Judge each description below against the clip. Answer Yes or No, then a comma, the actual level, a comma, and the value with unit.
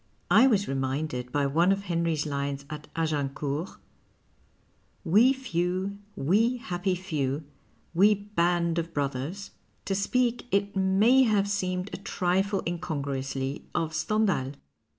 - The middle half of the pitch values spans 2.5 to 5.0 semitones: No, wide, 5.5 semitones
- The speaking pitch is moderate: Yes, medium, 175 Hz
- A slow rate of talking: Yes, slow, 120 wpm